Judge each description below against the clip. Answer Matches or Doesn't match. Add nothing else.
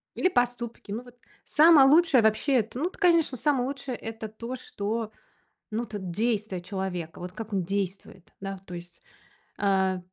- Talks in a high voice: Matches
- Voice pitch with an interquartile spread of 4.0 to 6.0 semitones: Matches